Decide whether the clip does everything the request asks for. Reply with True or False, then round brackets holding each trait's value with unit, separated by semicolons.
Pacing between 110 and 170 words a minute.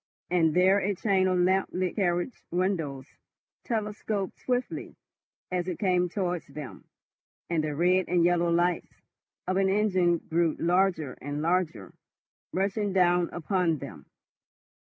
True (135 wpm)